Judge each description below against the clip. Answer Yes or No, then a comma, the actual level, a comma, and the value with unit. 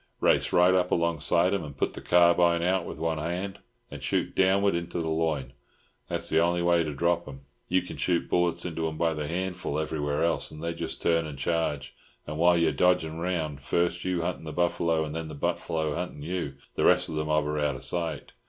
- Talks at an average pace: No, fast, 225 wpm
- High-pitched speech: No, very low, 85 Hz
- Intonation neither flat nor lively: No, narrow, 2.1 semitones